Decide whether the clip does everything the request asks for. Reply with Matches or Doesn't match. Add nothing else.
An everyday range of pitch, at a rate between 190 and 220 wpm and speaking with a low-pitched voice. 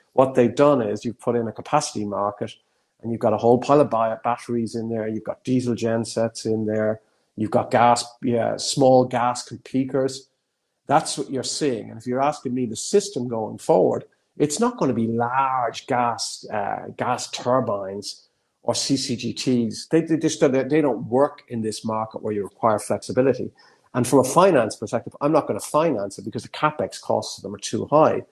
Matches